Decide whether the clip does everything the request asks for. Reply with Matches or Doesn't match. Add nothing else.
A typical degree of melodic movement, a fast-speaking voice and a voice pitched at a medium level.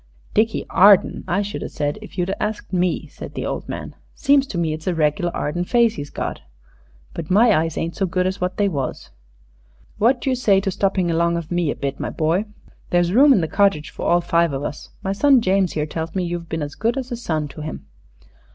Matches